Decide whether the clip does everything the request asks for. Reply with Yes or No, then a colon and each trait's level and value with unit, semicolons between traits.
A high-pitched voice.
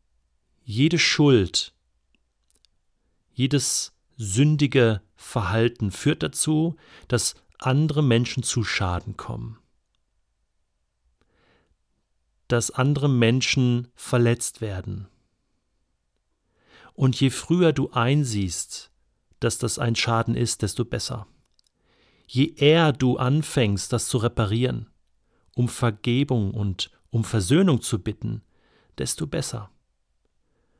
No: low, 120 Hz